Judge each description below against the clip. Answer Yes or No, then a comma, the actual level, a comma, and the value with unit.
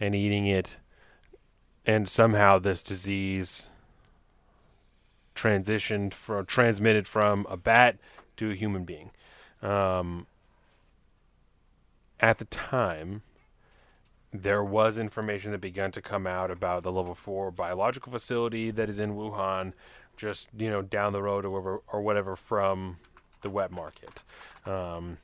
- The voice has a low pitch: Yes, low, 100 Hz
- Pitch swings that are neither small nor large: No, narrow, 2.1 semitones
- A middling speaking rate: No, slow, 130 wpm